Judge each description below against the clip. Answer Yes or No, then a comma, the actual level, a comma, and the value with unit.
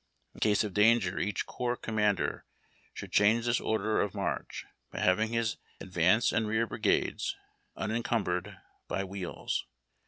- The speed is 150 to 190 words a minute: No, slow, 135 wpm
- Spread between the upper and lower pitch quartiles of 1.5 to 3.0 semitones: Yes, average, 2.7 semitones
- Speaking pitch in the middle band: No, low, 105 Hz